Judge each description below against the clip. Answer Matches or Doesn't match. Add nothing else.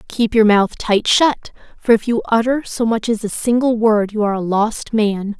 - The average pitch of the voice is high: Matches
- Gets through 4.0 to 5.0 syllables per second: Matches